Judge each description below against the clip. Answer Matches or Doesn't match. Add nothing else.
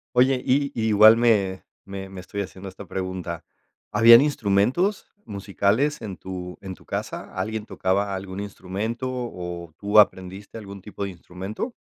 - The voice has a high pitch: Doesn't match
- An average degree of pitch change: Matches